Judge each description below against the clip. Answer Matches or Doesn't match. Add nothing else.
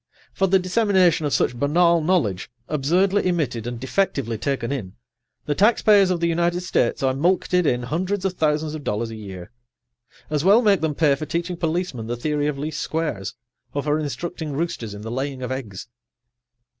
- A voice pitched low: Doesn't match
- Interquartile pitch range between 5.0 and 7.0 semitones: Matches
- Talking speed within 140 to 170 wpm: Doesn't match